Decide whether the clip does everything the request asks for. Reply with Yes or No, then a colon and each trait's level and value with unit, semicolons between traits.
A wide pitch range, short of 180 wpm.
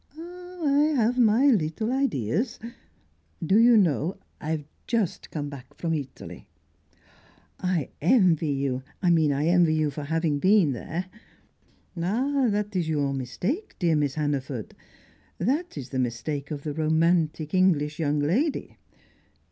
Yes: wide, 7.0 semitones; average, 140 wpm